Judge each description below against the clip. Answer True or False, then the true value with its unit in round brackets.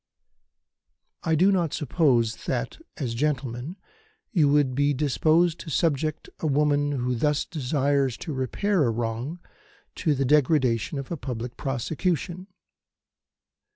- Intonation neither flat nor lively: True (3.9 semitones)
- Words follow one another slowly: True (125 wpm)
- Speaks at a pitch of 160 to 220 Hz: False (145 Hz)